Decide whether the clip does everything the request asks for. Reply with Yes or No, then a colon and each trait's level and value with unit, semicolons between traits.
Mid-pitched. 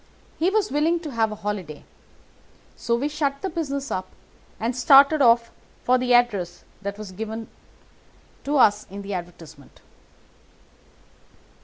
No: high, 235 Hz